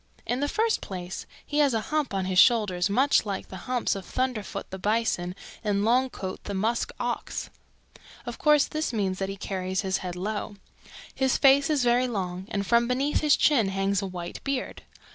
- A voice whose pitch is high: Yes, high, 215 Hz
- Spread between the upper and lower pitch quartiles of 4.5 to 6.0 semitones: Yes, average, 5.3 semitones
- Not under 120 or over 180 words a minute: No, average, 190 wpm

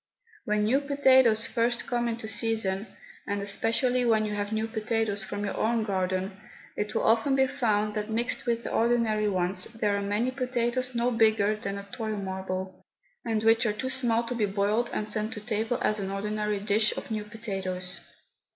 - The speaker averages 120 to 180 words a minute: No, average, 190 wpm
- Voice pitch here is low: No, high, 215 Hz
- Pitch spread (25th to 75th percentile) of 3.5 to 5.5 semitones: No, narrow, 2.5 semitones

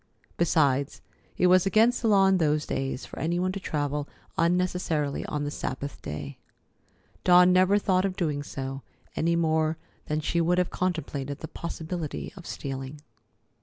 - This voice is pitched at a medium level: Yes, medium, 160 Hz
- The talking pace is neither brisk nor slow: Yes, average, 160 wpm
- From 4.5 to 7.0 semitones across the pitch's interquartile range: No, average, 4.0 semitones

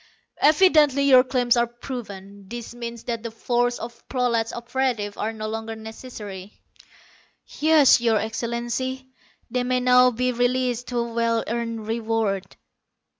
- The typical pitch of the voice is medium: No, high, 235 Hz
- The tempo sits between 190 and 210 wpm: No, slow, 135 wpm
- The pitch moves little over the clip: Yes, narrow, 2.1 semitones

